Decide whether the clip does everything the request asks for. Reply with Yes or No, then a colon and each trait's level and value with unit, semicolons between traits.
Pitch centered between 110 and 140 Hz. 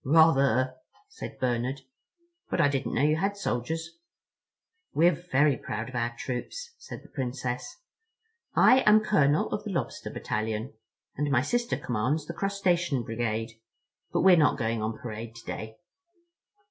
Yes: low, 135 Hz